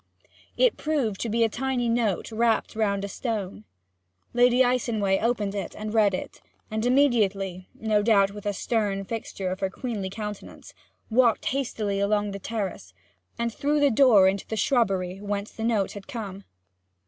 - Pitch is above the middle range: Yes, high, 215 Hz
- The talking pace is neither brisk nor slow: Yes, average, 165 wpm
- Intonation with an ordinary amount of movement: Yes, average, 3.0 semitones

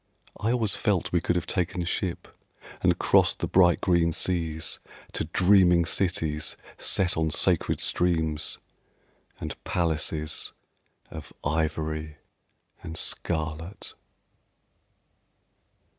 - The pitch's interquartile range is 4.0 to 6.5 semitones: No, narrow, 2.5 semitones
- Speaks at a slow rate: Yes, slow, 100 wpm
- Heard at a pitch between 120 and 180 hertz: No, very low, 85 Hz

